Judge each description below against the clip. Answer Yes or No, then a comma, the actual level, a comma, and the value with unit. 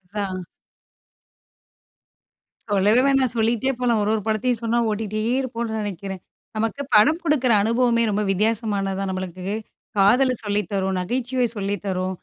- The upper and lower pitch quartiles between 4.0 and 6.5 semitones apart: No, average, 3.5 semitones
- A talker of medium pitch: No, high, 215 Hz